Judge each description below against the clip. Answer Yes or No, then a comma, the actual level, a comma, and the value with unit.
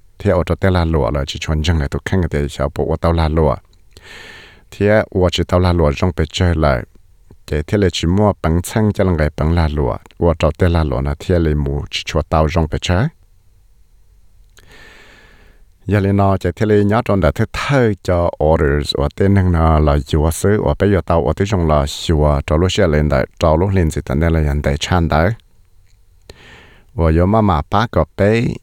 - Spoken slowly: Yes, slow, 110 wpm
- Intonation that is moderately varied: Yes, average, 3.6 semitones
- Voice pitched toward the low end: Yes, very low, 85 Hz